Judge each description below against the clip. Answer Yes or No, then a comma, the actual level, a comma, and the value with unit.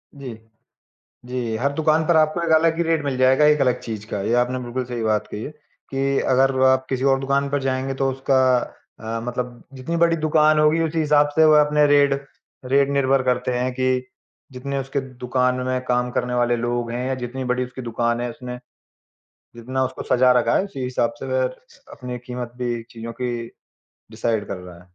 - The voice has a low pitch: Yes, low, 130 Hz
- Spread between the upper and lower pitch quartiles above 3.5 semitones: No, narrow, 2.5 semitones